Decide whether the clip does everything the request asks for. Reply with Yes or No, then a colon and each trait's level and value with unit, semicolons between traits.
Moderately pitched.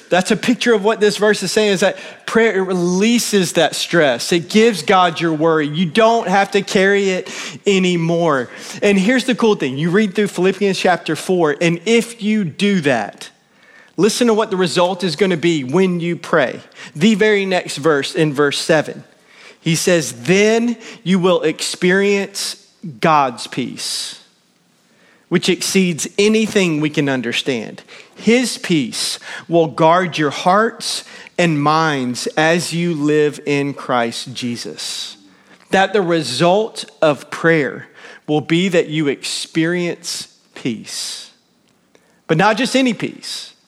Yes: medium, 180 Hz